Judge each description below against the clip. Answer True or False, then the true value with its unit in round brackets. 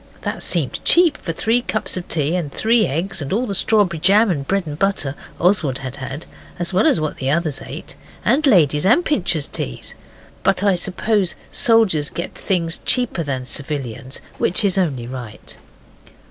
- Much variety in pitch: True (6.2 semitones)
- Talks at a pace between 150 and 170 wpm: False (185 wpm)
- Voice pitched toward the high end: False (175 Hz)